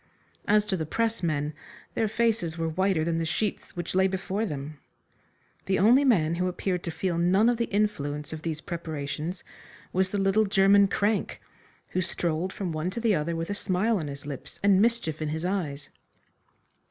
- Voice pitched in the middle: Yes, medium, 180 Hz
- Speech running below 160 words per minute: No, average, 185 wpm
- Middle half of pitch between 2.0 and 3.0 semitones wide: No, average, 4.2 semitones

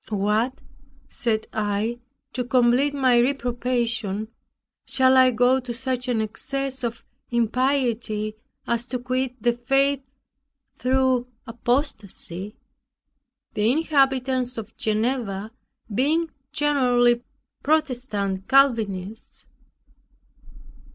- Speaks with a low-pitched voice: No, high, 245 Hz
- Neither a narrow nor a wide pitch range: Yes, average, 3.0 semitones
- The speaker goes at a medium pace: No, slow, 90 wpm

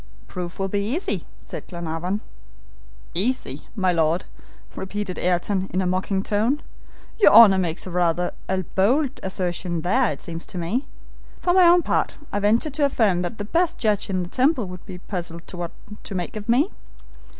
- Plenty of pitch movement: No, average, 4.7 semitones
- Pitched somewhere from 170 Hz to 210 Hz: Yes, high, 190 Hz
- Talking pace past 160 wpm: Yes, average, 170 wpm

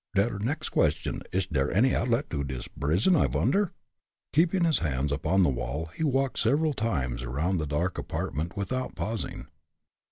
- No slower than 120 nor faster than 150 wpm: No, average, 165 wpm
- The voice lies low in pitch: Yes, very low, 95 Hz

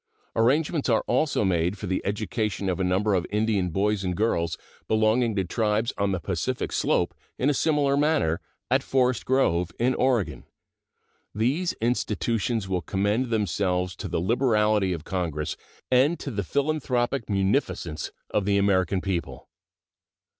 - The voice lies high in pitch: No, low, 105 Hz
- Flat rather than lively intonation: No, average, 5.0 semitones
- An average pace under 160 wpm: Yes, average, 145 wpm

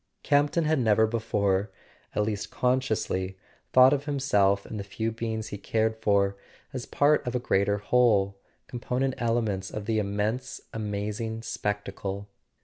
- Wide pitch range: No, average, 3.4 semitones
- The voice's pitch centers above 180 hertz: No, low, 110 Hz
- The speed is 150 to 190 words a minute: No, average, 140 wpm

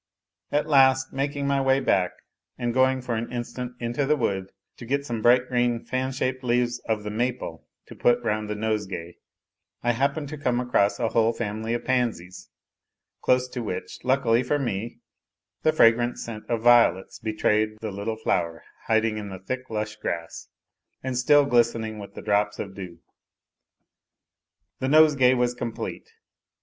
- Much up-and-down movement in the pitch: No, average, 3.2 semitones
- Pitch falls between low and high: No, low, 120 Hz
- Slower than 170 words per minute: Yes, average, 160 wpm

